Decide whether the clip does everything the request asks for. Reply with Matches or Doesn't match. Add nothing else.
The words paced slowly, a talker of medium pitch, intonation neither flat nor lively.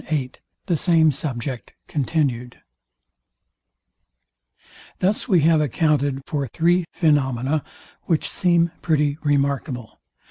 Matches